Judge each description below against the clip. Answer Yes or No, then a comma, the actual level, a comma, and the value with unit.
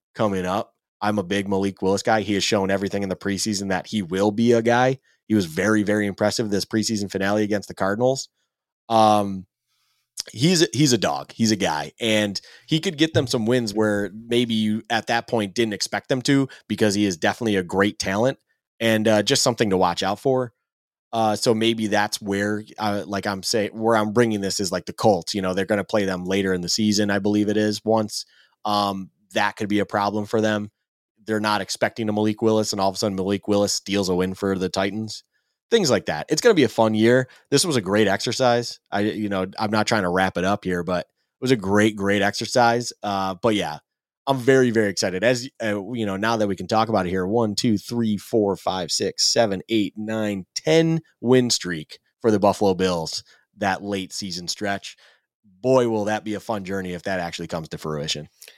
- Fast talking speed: Yes, fast, 220 wpm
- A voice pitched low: Yes, low, 105 Hz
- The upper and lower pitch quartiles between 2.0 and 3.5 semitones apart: Yes, narrow, 2.6 semitones